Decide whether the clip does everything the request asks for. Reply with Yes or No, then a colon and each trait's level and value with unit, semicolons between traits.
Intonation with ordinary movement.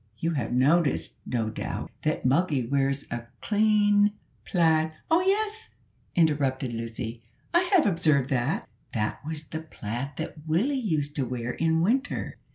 No: wide, 7.2 semitones